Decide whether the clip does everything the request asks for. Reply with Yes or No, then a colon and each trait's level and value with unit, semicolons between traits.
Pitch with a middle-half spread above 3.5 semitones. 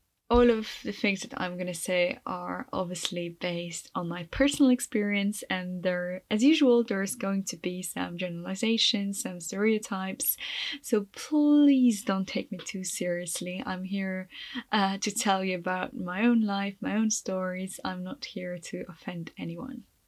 Yes: average, 4.0 semitones